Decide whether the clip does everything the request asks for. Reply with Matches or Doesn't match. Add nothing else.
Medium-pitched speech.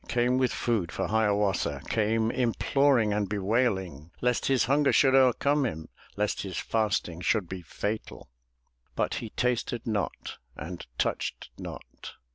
Doesn't match